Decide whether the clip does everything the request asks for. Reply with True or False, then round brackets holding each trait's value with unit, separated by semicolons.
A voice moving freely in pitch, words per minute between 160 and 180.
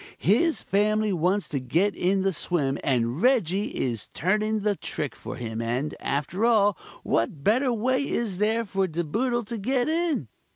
True (7.1 semitones; 170 wpm)